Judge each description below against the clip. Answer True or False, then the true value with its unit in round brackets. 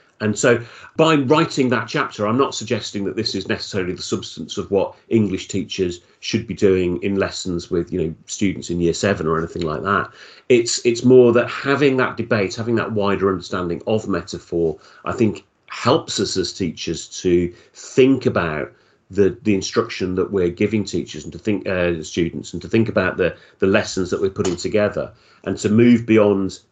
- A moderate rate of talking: True (190 wpm)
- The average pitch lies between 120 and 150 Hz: False (105 Hz)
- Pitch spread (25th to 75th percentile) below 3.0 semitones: False (4.6 semitones)